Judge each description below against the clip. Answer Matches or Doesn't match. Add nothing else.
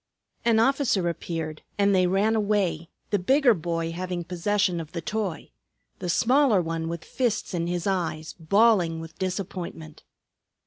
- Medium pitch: Matches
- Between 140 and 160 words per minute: Matches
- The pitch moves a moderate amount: Matches